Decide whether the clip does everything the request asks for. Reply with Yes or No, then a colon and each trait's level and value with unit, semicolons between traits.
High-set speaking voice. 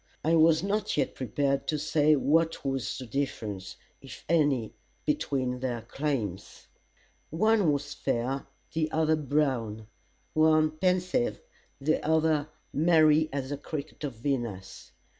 No: medium, 145 Hz